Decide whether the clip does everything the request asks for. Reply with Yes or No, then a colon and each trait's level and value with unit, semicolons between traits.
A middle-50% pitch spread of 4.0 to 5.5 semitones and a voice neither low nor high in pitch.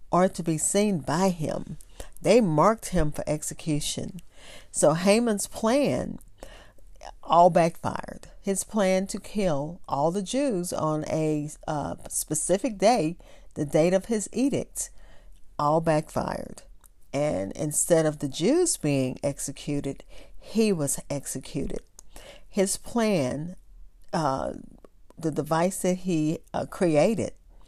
Yes: average, 4.6 semitones; medium, 170 Hz